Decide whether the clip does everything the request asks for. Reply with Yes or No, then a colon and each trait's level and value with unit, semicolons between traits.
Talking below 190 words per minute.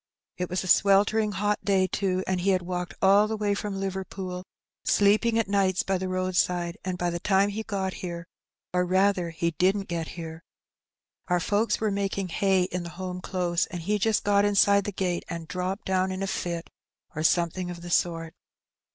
No: average, 200 wpm